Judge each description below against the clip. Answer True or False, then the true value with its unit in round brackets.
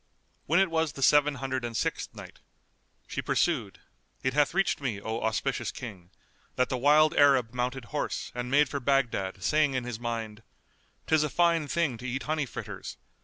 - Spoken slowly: False (180 wpm)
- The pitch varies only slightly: False (3.7 semitones)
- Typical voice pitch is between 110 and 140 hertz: True (135 Hz)